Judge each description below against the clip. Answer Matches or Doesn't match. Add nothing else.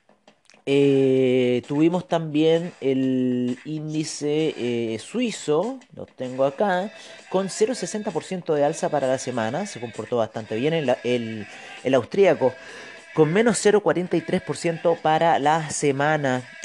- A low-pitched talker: Doesn't match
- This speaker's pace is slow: Matches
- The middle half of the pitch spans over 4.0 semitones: Matches